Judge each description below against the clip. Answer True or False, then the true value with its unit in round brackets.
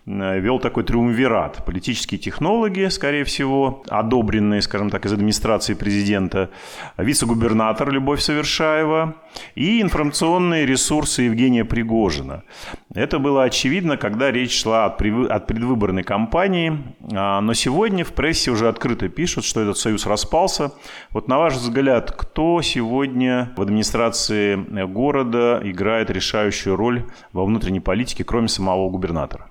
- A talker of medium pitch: False (120 Hz)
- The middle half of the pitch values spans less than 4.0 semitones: False (5.2 semitones)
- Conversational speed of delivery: True (120 wpm)